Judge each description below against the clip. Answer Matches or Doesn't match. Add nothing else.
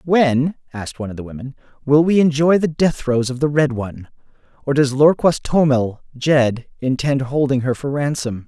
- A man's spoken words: Matches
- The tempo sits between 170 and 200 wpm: Matches